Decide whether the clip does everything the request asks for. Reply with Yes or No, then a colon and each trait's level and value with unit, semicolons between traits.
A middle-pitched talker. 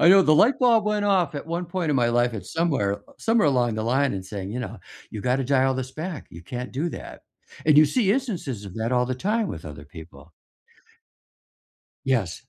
No: low, 130 Hz